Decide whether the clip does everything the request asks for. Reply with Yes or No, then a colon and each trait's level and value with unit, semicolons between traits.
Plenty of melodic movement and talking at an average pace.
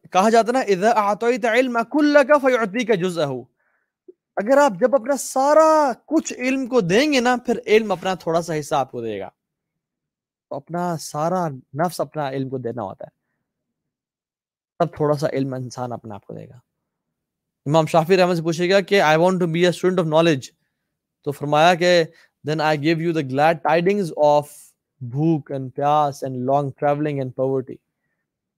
Yes: wide, 7.7 semitones; average, 175 wpm